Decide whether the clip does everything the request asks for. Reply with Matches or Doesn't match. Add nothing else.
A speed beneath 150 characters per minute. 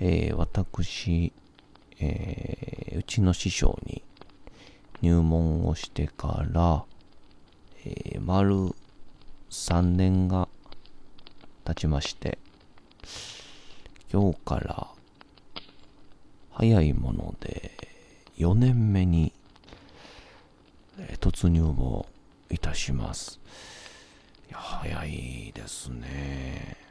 Matches